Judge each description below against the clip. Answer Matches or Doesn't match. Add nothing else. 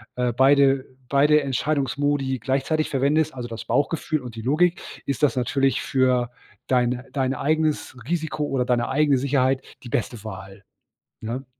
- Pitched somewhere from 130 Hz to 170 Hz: Matches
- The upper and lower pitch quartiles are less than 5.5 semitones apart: Matches